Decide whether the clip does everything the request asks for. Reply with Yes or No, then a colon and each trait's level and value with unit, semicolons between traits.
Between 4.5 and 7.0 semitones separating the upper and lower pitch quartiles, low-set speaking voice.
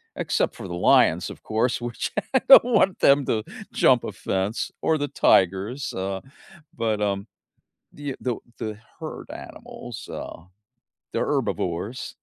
Yes: average, 4.8 semitones; low, 110 Hz